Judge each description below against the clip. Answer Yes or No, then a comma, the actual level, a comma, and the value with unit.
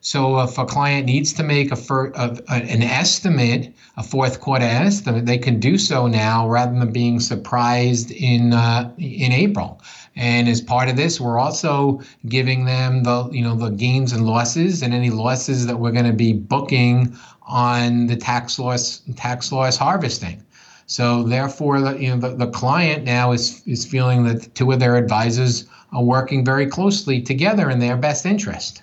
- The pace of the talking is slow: No, average, 185 wpm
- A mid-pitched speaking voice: No, low, 125 Hz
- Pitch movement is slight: Yes, narrow, 2.1 semitones